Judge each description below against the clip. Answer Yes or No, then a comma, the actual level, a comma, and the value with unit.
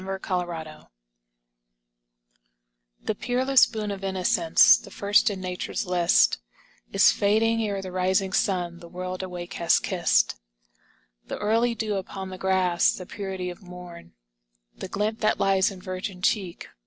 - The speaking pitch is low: No, high, 190 Hz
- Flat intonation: Yes, narrow, 2.3 semitones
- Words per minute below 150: Yes, average, 140 wpm